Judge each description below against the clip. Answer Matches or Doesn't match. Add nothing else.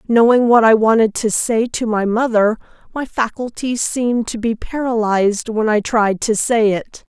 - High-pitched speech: Matches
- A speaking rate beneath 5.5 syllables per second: Matches